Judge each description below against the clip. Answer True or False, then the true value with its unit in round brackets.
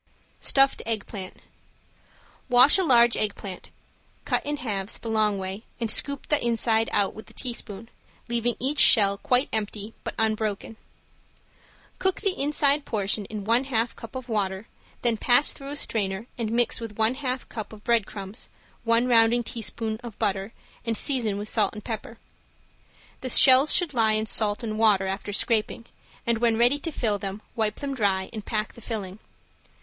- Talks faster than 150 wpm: True (175 wpm)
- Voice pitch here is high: True (225 Hz)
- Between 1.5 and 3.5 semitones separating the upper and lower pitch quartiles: True (2.8 semitones)